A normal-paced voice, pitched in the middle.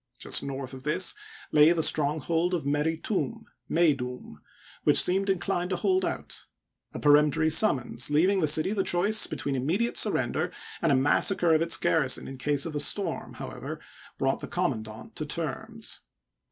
Yes: average, 165 wpm; medium, 160 Hz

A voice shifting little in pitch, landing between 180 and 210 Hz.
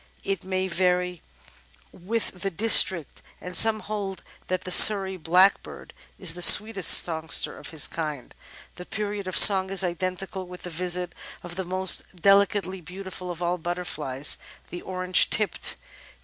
Yes: narrow, 1.8 semitones; medium, 185 Hz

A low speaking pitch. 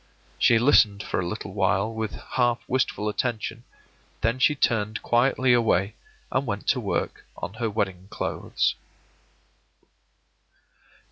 Yes: low, 110 Hz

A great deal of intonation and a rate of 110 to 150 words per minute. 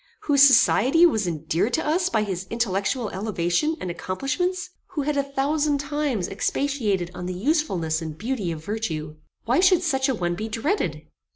No: wide, 8.1 semitones; average, 170 wpm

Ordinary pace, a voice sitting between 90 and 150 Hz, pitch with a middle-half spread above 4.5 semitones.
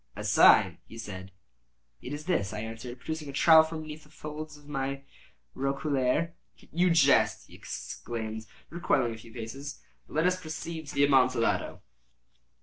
Yes: average, 160 wpm; medium, 140 Hz; average, 4.9 semitones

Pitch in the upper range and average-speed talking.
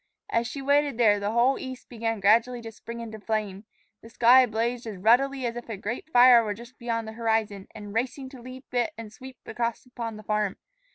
No: high, 230 Hz; fast, 215 wpm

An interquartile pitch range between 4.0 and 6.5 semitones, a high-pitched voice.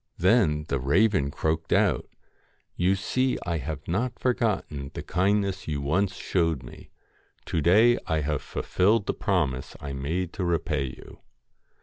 No: average, 5.0 semitones; very low, 85 Hz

